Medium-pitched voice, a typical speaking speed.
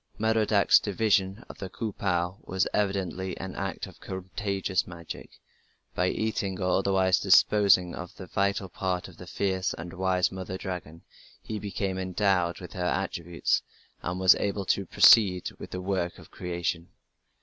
No: very low, 95 Hz; average, 155 wpm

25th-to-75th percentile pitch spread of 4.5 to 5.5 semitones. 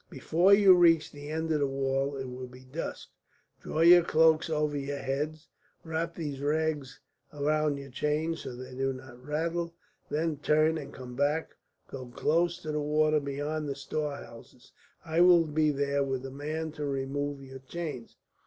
No: average, 2.7 semitones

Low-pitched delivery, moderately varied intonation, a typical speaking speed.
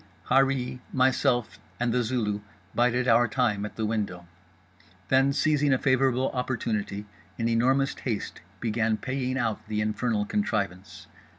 No: low, 115 Hz; average, 3.8 semitones; slow, 125 wpm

